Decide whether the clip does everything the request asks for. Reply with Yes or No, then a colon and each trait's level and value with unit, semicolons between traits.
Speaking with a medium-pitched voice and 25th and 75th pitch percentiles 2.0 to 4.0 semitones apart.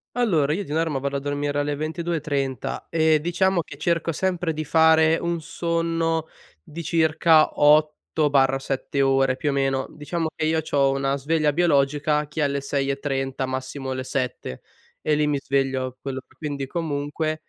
Yes: medium, 150 Hz; average, 2.8 semitones